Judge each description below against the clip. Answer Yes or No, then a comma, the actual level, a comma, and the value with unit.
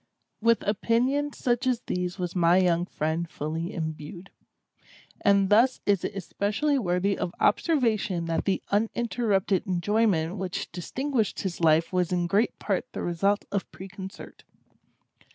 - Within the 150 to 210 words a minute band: No, slow, 135 wpm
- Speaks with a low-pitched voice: No, high, 195 Hz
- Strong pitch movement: No, average, 4.3 semitones